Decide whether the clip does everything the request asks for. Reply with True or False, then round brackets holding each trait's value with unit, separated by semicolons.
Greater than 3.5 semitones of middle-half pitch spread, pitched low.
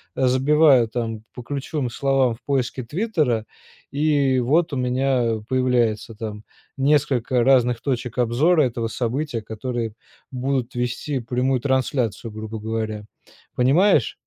False (2.9 semitones; 125 Hz)